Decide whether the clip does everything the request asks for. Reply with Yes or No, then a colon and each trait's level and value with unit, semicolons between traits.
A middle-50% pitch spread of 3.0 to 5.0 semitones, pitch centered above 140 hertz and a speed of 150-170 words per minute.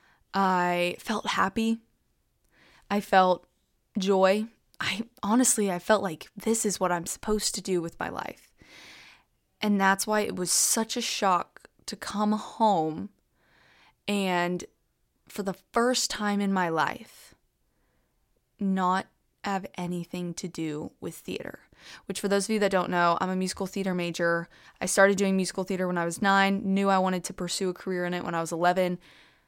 No: narrow, 2.5 semitones; high, 190 Hz; average, 165 wpm